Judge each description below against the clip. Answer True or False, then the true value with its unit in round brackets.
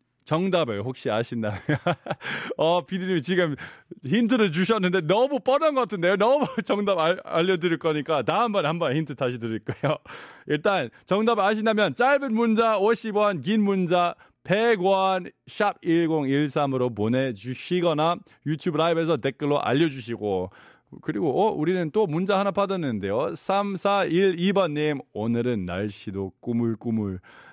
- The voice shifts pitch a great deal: True (6.5 semitones)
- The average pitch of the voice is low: False (170 Hz)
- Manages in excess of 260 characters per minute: True (280 characters per minute)